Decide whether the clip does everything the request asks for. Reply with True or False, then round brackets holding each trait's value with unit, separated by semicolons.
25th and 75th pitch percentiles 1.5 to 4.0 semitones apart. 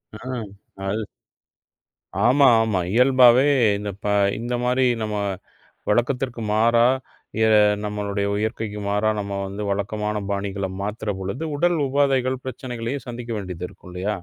True (3.4 semitones)